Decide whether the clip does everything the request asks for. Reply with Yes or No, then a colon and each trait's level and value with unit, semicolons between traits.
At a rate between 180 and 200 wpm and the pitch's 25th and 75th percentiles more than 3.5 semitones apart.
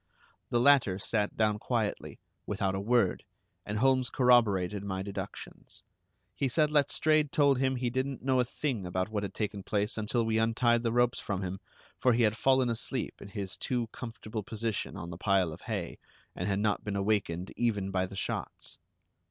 Yes: average, 185 wpm; average, 3.9 semitones